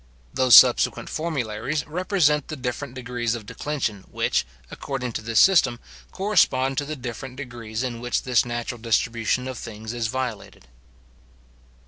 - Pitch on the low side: Yes, low, 125 Hz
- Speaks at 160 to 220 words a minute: No, average, 140 wpm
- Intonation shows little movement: No, average, 3.3 semitones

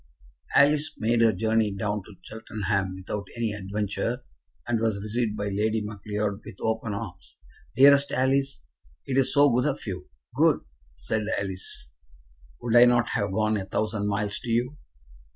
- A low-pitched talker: Yes, low, 110 Hz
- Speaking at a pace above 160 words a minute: No, average, 155 wpm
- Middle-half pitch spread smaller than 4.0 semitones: Yes, average, 2.9 semitones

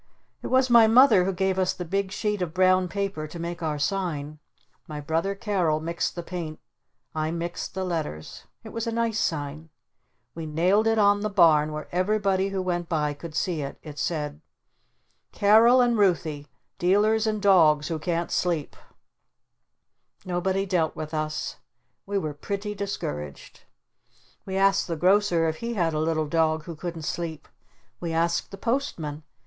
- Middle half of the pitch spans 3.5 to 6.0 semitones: Yes, average, 4.1 semitones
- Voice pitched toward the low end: No, medium, 175 Hz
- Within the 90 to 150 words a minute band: No, average, 165 wpm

